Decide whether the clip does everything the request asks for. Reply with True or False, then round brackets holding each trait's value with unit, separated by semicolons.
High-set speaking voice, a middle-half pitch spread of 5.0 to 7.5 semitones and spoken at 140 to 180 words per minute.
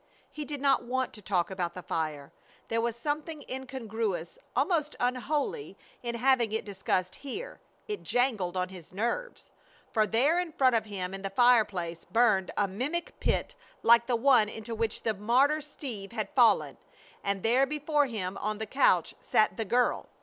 True (230 Hz; 5.3 semitones; 170 wpm)